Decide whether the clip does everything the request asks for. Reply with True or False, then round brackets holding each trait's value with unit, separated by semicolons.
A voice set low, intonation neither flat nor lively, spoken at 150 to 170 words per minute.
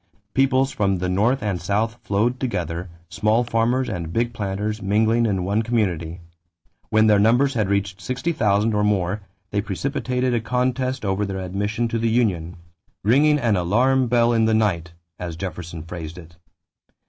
True (105 Hz; 4.1 semitones; 165 wpm)